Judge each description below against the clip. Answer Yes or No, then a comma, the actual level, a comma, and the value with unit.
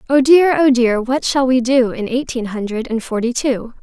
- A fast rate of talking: Yes, fast, 220 wpm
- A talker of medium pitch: No, very high, 250 Hz